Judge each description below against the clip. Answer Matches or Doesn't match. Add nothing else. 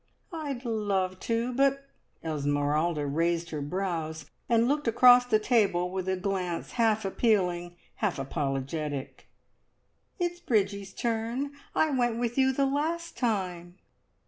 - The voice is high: Matches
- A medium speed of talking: Doesn't match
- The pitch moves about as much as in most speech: Doesn't match